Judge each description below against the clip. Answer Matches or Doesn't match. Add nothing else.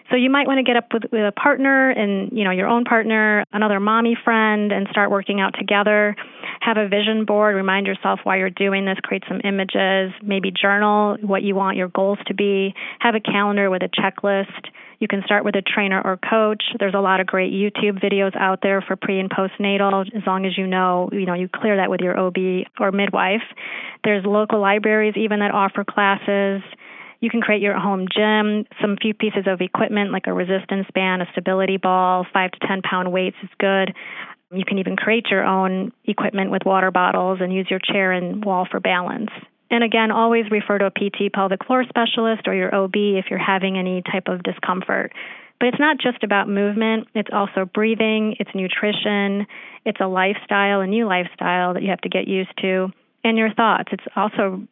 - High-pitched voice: Matches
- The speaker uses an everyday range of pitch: Doesn't match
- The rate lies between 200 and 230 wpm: Matches